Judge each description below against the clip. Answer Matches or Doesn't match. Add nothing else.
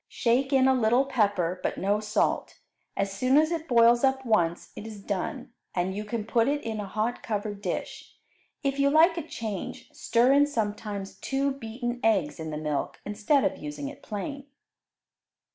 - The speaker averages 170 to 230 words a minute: Matches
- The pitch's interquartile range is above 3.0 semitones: Matches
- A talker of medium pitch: Doesn't match